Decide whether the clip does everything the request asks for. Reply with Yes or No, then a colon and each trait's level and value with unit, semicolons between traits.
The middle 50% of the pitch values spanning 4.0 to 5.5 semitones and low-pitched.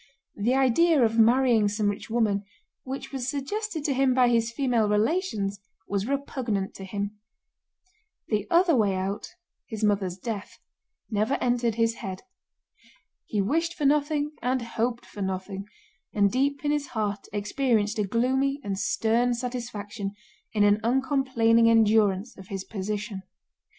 No: average, 4.4 semitones; high, 230 Hz